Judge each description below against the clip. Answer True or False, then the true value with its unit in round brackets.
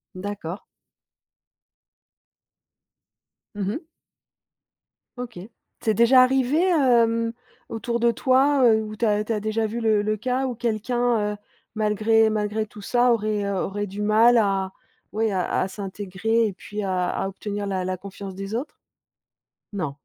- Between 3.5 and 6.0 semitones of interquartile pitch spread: False (2.7 semitones)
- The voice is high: True (215 Hz)